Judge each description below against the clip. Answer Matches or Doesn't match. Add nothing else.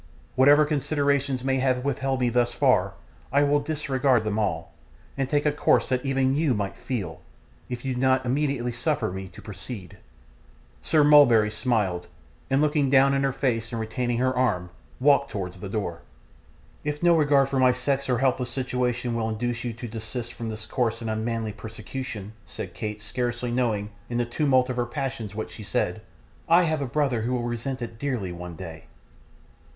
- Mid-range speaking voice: Doesn't match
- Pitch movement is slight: Doesn't match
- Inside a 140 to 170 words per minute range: Doesn't match